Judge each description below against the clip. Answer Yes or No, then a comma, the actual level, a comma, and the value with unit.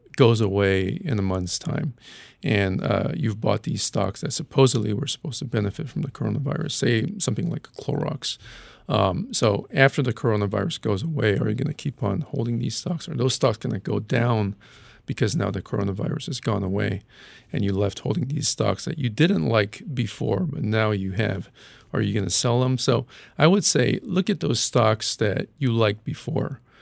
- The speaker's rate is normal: Yes, average, 195 wpm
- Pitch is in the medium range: No, low, 120 Hz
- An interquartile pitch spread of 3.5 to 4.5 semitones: No, wide, 5.6 semitones